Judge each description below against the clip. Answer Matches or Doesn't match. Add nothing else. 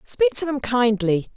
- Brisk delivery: Doesn't match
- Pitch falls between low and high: Doesn't match